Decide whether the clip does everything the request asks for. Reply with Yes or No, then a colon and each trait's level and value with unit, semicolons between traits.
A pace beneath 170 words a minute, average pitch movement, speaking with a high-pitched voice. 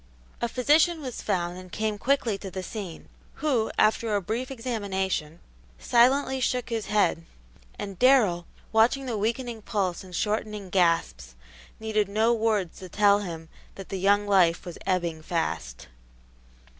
Yes: average, 145 wpm; average, 4.2 semitones; high, 205 Hz